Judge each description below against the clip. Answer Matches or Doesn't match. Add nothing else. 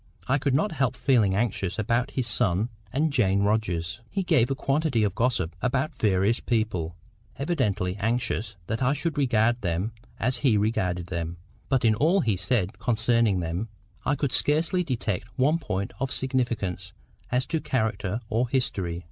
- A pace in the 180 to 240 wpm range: Doesn't match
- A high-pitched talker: Doesn't match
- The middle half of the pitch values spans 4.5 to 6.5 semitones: Matches